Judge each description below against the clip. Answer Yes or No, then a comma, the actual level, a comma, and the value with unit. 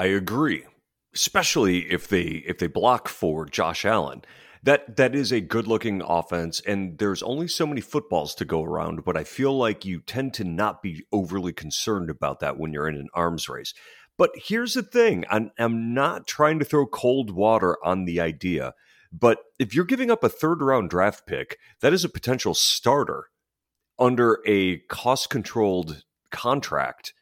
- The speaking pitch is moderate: No, low, 110 Hz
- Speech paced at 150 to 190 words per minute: Yes, average, 180 wpm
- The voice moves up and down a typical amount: No, wide, 7.5 semitones